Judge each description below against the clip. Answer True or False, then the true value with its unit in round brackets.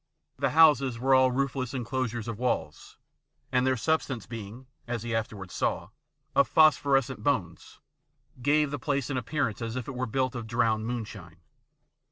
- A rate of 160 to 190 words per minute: True (165 wpm)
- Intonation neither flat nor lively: True (3.0 semitones)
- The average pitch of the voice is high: False (125 Hz)